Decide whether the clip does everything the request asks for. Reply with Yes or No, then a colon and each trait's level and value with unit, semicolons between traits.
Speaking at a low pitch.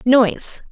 No: high, 245 Hz